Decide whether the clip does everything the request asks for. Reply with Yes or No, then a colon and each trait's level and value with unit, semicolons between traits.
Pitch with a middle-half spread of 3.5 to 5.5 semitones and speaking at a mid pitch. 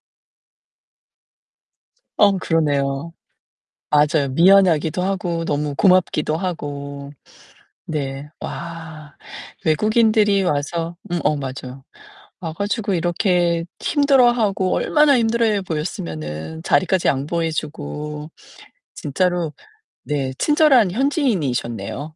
Yes: average, 5.1 semitones; medium, 165 Hz